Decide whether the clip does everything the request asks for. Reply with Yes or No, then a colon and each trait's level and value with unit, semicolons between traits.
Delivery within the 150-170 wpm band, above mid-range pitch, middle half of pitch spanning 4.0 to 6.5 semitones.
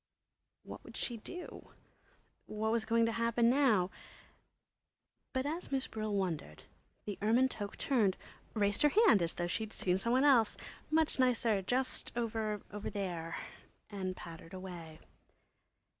No: average, 140 wpm; high, 215 Hz; average, 4.4 semitones